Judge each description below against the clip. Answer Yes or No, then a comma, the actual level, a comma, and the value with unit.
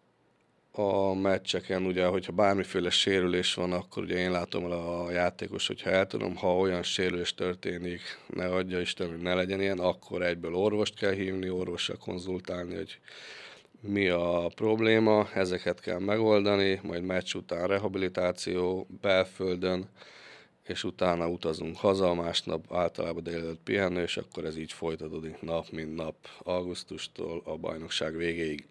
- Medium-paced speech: Yes, average, 140 wpm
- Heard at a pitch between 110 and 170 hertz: No, very low, 90 Hz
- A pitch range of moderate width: No, narrow, 1.7 semitones